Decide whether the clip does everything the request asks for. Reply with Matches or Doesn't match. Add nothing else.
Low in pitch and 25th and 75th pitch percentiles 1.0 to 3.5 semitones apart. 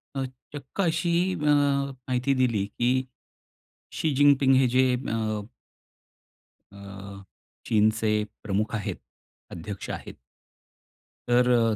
Doesn't match